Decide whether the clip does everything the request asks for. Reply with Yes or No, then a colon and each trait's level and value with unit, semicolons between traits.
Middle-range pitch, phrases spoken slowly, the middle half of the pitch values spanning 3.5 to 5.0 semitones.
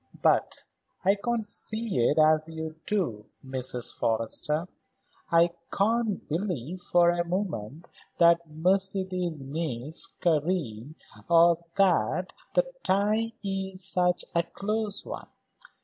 Yes: medium, 175 Hz; slow, 110 wpm; average, 4.0 semitones